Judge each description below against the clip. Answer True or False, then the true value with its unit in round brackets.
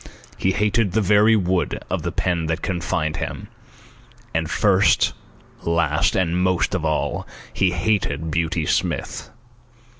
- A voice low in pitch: True (90 Hz)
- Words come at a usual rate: False (130 wpm)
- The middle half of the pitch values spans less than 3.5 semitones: True (2.9 semitones)